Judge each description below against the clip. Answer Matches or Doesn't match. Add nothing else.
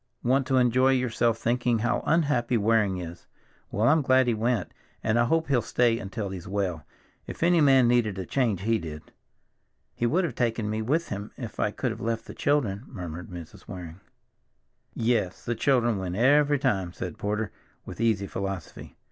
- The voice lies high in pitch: Doesn't match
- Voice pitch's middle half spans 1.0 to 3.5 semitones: Doesn't match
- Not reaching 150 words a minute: Doesn't match